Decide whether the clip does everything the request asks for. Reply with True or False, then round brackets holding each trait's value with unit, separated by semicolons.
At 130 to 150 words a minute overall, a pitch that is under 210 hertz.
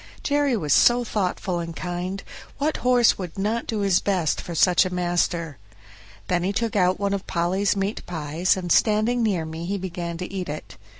False (190 wpm; 185 Hz)